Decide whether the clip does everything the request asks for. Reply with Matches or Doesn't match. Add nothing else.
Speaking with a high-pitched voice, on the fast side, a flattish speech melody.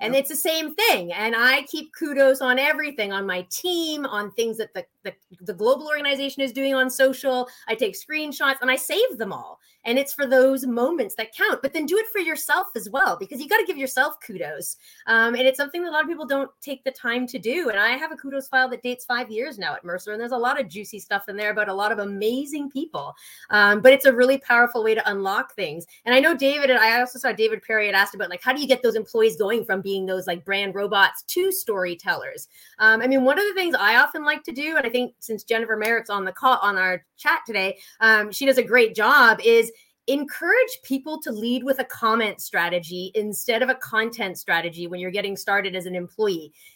Doesn't match